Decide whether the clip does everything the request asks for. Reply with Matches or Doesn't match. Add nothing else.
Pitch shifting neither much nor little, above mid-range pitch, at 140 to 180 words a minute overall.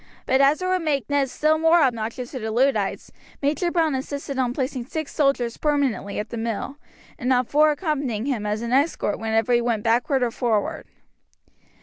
Doesn't match